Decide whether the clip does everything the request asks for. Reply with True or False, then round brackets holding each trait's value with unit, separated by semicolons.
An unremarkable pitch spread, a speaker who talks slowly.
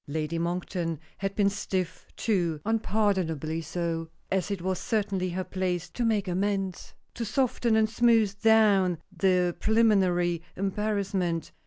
True (3.3 semitones; 130 wpm)